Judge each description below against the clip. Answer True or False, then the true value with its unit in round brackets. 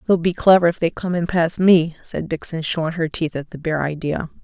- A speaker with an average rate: False (245 wpm)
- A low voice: False (165 Hz)